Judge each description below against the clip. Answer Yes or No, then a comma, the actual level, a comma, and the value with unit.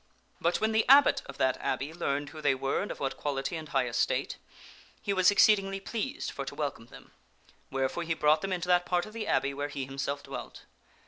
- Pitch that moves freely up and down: Yes, wide, 5.9 semitones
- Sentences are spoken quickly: Yes, fast, 215 wpm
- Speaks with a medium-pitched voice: Yes, medium, 155 Hz